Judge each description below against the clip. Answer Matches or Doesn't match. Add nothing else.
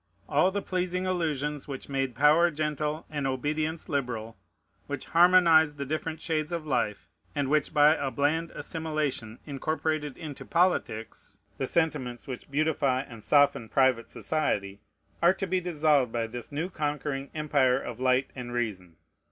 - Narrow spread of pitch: Doesn't match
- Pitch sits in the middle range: Matches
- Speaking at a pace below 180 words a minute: Matches